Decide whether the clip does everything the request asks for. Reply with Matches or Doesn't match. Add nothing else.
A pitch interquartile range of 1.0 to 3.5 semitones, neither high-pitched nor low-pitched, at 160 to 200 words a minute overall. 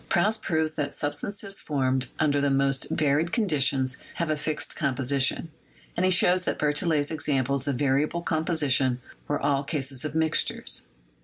Doesn't match